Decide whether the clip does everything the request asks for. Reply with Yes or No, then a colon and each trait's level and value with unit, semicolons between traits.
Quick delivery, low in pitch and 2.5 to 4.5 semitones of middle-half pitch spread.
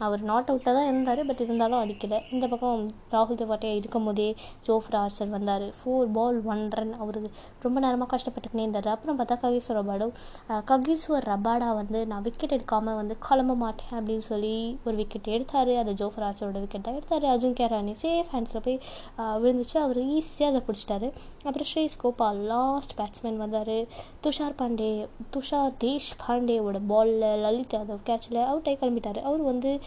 No: fast, 155 wpm; high, 230 Hz; average, 3.0 semitones